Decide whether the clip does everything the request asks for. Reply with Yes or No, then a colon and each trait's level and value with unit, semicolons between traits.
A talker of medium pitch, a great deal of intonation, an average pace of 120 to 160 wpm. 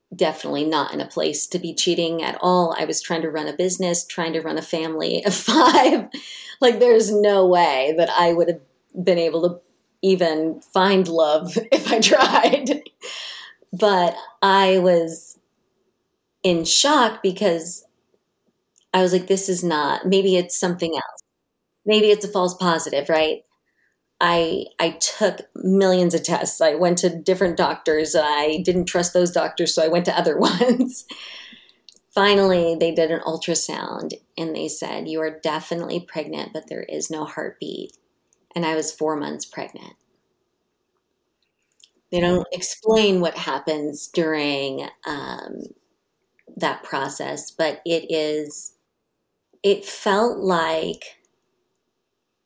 No: medium, 175 Hz; average, 3.0 semitones; average, 140 wpm